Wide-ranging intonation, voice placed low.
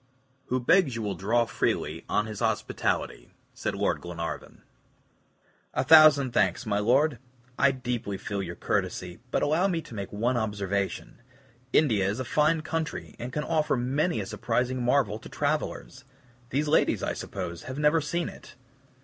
Yes: wide, 6.3 semitones; low, 125 Hz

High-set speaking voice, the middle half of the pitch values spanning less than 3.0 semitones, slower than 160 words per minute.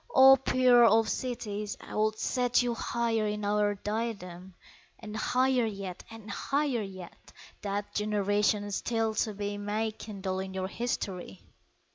Yes: high, 210 Hz; narrow, 2.4 semitones; average, 140 wpm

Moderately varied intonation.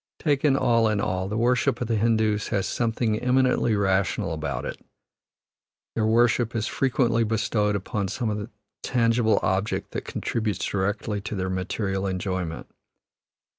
Yes: average, 3.0 semitones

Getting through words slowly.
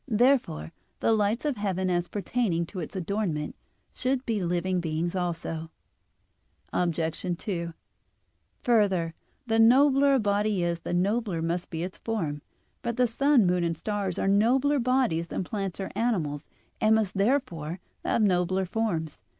No: average, 150 wpm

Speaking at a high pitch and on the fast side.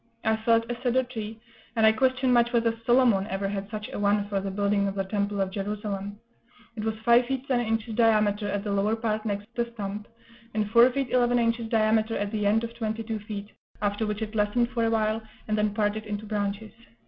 Yes: high, 215 Hz; fast, 220 wpm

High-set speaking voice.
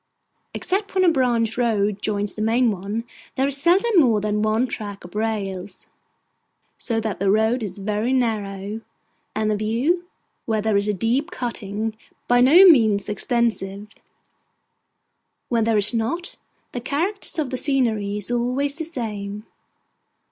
Yes: high, 225 Hz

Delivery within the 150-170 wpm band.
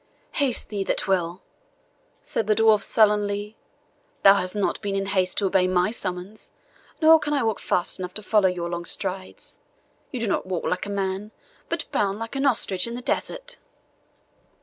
No: average, 180 wpm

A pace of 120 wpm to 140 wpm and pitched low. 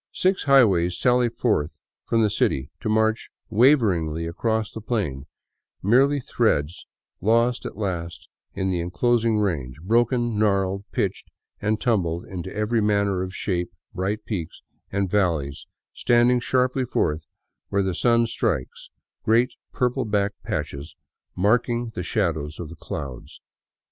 Yes: slow, 135 wpm; low, 105 Hz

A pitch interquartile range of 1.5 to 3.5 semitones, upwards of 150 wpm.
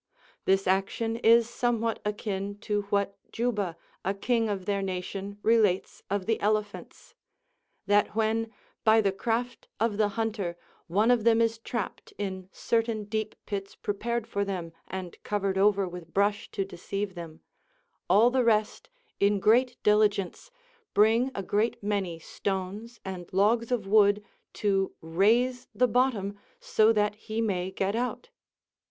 No: narrow, 2.6 semitones; average, 145 wpm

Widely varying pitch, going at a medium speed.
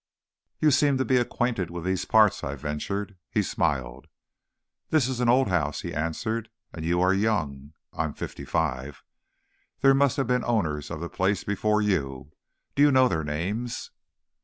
Yes: wide, 7.8 semitones; average, 175 wpm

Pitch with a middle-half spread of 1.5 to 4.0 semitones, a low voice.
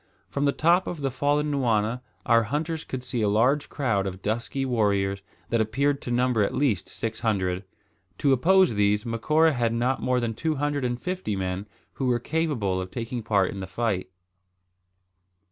No: average, 5.2 semitones; low, 120 Hz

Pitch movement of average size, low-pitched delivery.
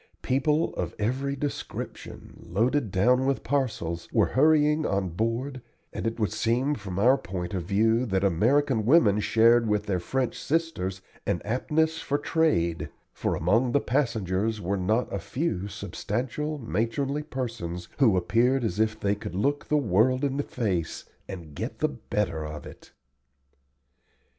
No: wide, 6.0 semitones; low, 115 Hz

